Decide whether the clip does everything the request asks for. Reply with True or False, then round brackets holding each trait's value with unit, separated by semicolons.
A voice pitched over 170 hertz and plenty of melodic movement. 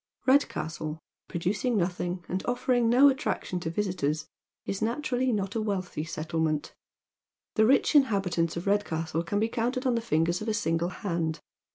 True (190 Hz; 5.8 semitones)